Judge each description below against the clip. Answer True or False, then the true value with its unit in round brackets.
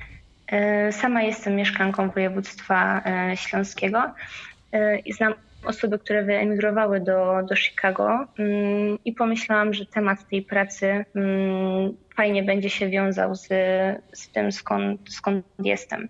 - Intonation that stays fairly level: True (1.7 semitones)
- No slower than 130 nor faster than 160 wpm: False (110 wpm)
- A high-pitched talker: True (195 Hz)